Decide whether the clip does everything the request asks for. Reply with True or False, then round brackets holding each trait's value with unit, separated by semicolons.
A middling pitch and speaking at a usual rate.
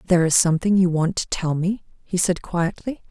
False (180 Hz; 215 wpm)